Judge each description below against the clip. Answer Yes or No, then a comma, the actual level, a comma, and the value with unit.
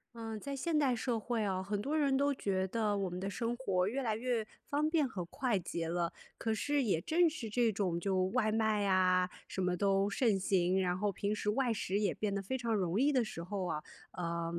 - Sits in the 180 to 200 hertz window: No, high, 210 Hz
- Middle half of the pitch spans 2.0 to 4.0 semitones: No, average, 4.6 semitones